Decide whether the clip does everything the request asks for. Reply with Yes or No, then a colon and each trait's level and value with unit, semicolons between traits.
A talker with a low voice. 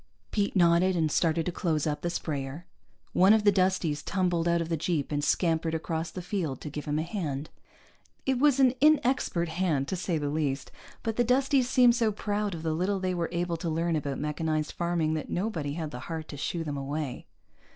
No: medium, 170 Hz